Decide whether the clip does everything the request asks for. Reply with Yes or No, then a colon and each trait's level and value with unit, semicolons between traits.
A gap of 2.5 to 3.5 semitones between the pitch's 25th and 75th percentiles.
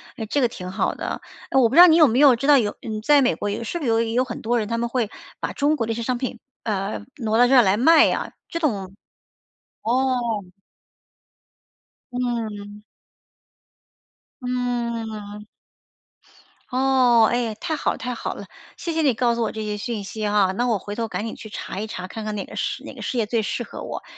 Yes: average, 3.0 semitones